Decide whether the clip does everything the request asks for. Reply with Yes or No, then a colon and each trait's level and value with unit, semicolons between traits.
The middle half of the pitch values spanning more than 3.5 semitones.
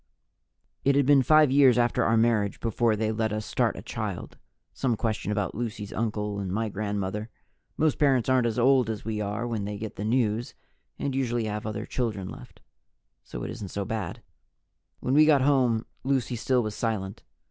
No: average, 3.2 semitones